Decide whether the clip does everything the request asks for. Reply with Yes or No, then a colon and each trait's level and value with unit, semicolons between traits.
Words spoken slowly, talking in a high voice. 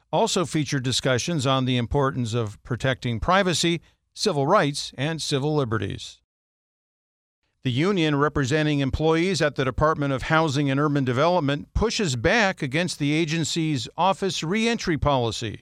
No: slow, 130 wpm; medium, 145 Hz